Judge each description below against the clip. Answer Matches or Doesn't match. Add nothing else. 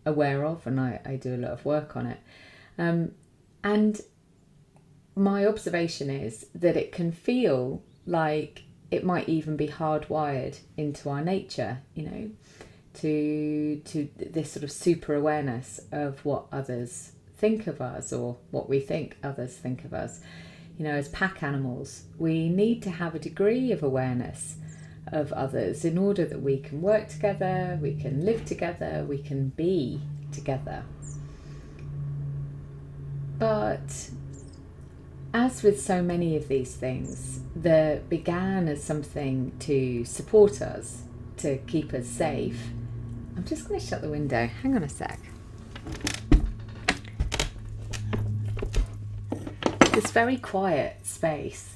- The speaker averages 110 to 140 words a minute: Matches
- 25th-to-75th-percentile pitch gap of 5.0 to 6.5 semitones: Doesn't match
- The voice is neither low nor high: Matches